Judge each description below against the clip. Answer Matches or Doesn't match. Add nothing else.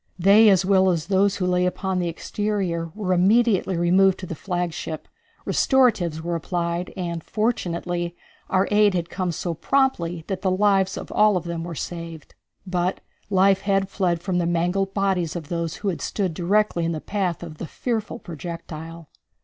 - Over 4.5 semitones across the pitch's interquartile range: Doesn't match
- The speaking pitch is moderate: Matches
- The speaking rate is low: Doesn't match